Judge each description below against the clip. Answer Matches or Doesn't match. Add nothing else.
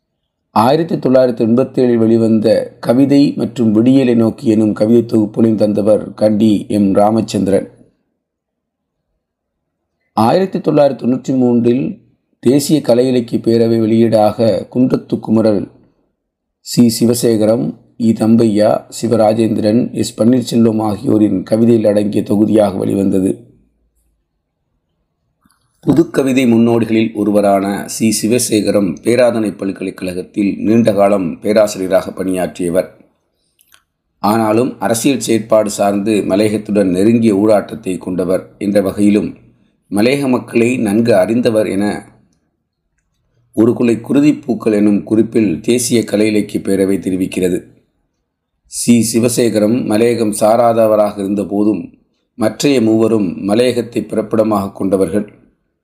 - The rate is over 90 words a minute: Doesn't match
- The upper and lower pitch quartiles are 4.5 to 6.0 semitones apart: Doesn't match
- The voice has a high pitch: Doesn't match